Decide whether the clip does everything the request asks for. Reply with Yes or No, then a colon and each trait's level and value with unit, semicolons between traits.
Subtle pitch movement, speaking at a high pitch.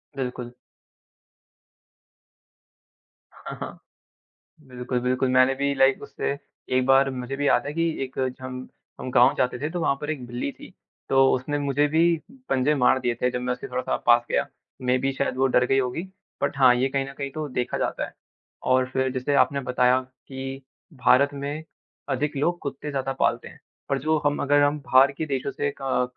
No: narrow, 1.8 semitones; low, 135 Hz